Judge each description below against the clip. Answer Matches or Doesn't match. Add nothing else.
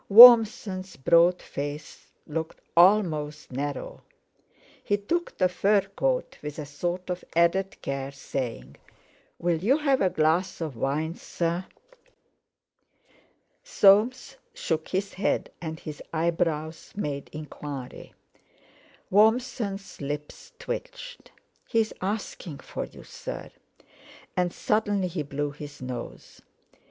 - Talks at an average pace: Doesn't match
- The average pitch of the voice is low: Doesn't match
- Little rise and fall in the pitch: Doesn't match